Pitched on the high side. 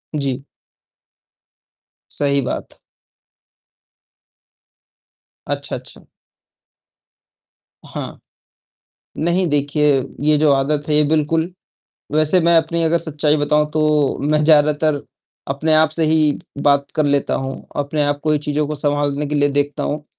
No: medium, 150 Hz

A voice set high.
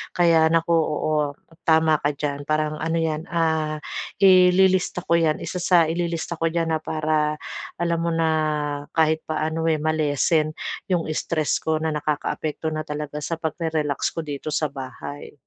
No: medium, 160 Hz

